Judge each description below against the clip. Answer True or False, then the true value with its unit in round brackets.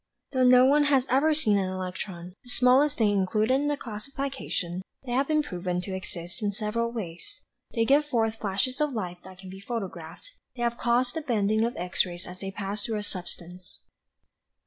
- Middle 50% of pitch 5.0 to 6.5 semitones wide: True (5.4 semitones)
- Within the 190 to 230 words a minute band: True (195 wpm)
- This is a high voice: True (215 Hz)